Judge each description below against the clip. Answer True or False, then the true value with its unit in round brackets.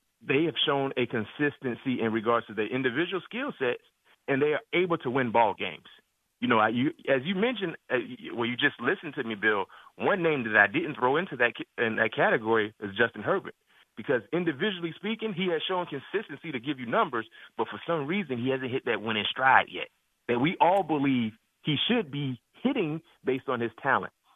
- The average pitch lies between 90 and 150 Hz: True (140 Hz)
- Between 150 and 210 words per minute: True (205 wpm)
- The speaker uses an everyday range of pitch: False (7.3 semitones)